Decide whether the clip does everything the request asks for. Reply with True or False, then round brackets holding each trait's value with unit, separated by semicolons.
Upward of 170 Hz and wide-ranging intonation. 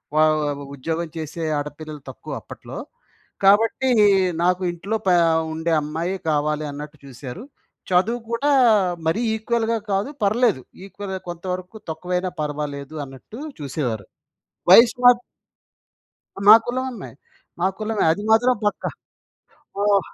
True (180 Hz; 6.3 semitones)